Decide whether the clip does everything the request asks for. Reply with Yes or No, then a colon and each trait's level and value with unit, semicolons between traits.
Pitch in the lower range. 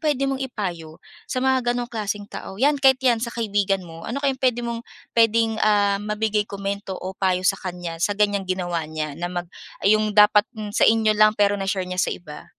No: high, 205 Hz